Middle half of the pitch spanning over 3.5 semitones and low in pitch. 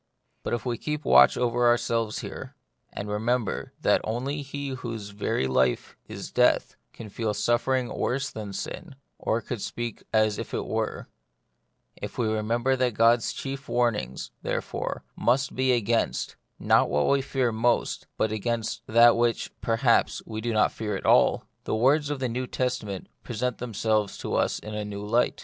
No: average, 2.7 semitones; low, 115 Hz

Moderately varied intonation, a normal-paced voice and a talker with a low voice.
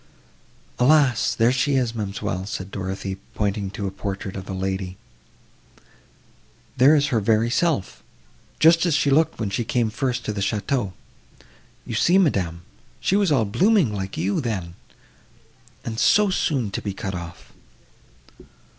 No: wide, 6.3 semitones; average, 145 wpm; low, 110 Hz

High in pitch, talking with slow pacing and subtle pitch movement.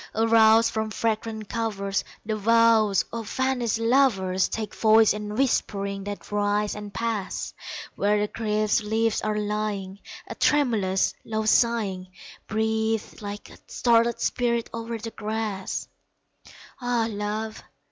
Yes: high, 220 Hz; slow, 125 wpm; narrow, 1.7 semitones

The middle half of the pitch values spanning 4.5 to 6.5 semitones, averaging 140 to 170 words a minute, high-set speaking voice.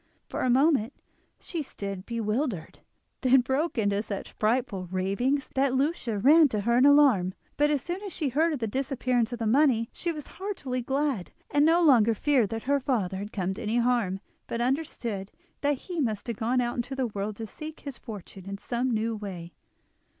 No: average, 5.0 semitones; average, 195 wpm; high, 245 Hz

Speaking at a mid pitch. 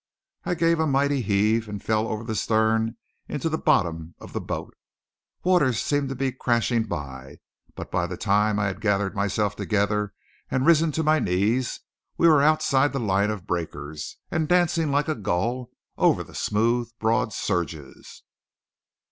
No: low, 110 Hz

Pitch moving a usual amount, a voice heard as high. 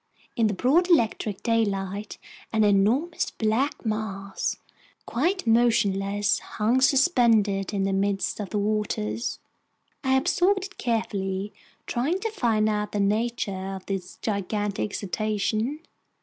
Yes: average, 3.4 semitones; high, 215 Hz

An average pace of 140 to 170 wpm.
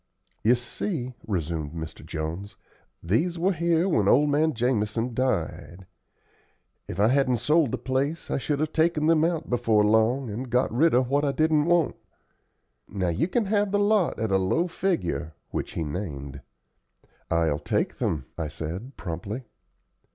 Yes: average, 160 wpm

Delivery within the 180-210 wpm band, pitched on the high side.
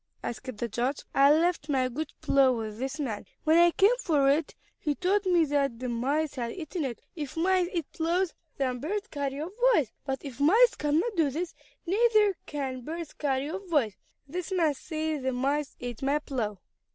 Yes: average, 190 wpm; very high, 295 Hz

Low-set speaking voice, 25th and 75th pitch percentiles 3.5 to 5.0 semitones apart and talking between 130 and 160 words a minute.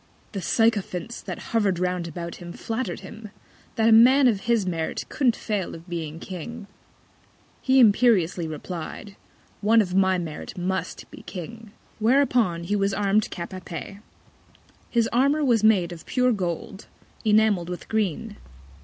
No: high, 200 Hz; average, 4.3 semitones; average, 150 wpm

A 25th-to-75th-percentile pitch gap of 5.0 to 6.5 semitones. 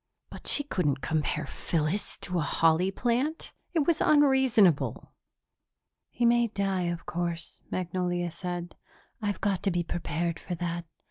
No: average, 4.6 semitones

